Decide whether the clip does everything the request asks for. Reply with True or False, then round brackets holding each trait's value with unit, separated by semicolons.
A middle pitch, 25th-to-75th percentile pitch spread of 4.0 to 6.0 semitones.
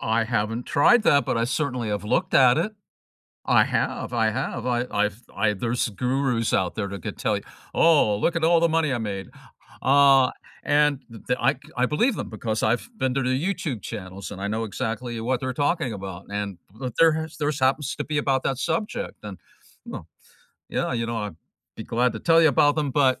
False (125 Hz; 5.0 semitones)